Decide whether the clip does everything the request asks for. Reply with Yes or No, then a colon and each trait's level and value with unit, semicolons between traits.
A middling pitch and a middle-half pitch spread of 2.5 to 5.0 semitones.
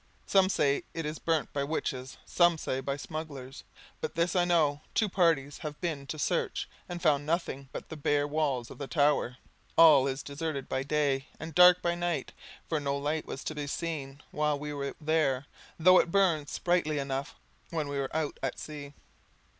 Yes: medium, 150 Hz; average, 2.9 semitones